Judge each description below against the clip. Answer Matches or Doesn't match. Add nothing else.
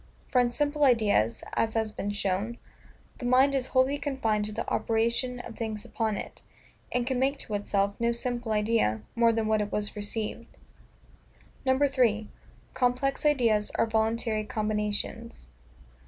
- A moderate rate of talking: Matches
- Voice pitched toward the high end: Matches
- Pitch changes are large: Doesn't match